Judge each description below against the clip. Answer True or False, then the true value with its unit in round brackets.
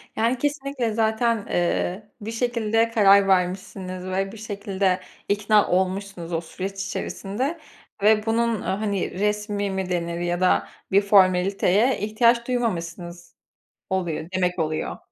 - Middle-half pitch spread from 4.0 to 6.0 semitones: False (3.3 semitones)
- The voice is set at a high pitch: True (200 Hz)